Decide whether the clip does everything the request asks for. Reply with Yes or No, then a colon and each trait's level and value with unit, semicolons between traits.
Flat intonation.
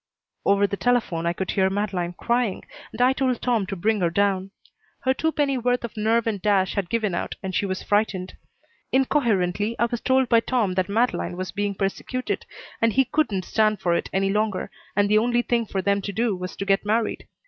No: average, 3.7 semitones